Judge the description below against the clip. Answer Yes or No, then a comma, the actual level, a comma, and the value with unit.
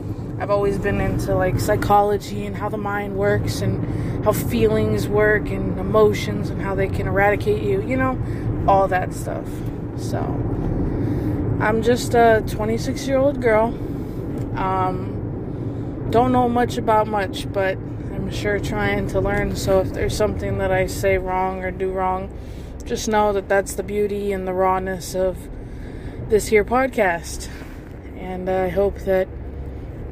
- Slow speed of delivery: No, average, 150 wpm